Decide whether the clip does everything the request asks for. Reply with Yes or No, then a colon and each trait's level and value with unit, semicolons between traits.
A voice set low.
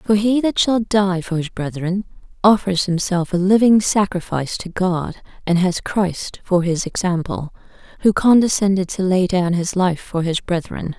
No: medium, 185 Hz